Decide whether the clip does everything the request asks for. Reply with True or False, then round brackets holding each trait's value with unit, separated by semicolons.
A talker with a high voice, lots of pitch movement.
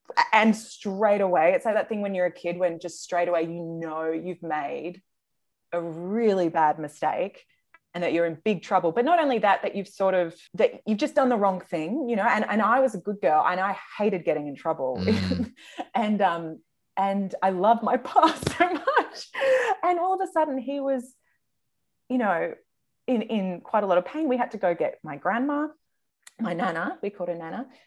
True (205 Hz; 7.2 semitones)